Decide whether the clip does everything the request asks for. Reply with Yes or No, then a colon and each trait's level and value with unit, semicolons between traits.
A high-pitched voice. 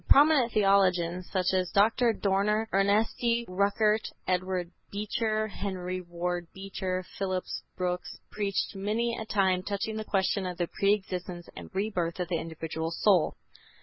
Yes: high, 195 Hz